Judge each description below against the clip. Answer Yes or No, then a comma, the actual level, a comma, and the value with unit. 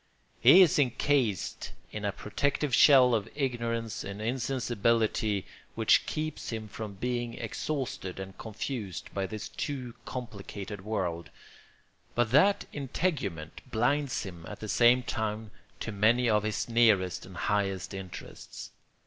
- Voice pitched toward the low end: Yes, low, 110 Hz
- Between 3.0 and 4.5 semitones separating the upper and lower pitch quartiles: Yes, average, 3.8 semitones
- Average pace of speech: No, slow, 130 wpm